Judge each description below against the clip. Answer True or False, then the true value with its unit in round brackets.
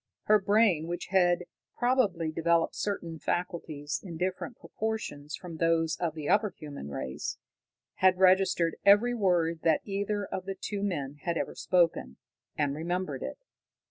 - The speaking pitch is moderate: True (175 Hz)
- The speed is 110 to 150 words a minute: True (145 wpm)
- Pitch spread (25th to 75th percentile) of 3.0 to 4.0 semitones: True (3.4 semitones)